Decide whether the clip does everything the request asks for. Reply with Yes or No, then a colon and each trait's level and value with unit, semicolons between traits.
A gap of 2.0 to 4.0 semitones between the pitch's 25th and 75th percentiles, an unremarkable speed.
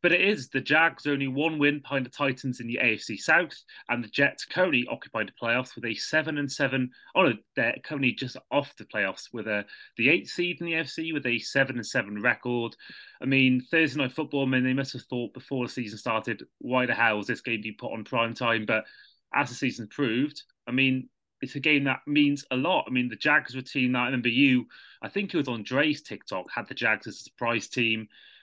No: average, 3.1 semitones; fast, 240 wpm